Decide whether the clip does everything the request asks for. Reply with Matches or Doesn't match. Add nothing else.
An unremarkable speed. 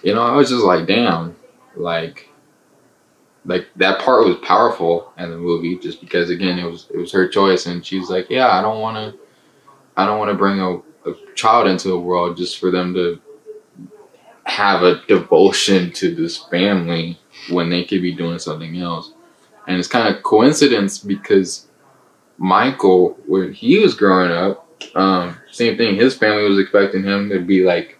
Matches